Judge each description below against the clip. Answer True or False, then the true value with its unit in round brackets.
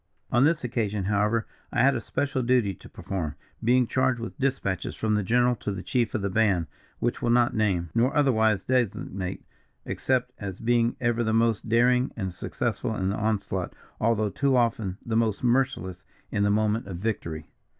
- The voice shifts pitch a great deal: False (3.6 semitones)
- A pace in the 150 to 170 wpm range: False (180 wpm)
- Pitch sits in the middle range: False (115 Hz)